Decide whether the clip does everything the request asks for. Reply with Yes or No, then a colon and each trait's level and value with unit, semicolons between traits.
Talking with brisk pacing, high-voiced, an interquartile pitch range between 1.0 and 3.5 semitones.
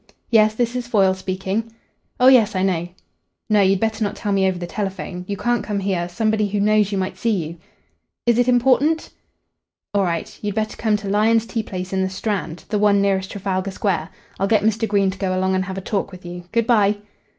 Yes: fast, 220 wpm; high, 200 Hz; narrow, 2.6 semitones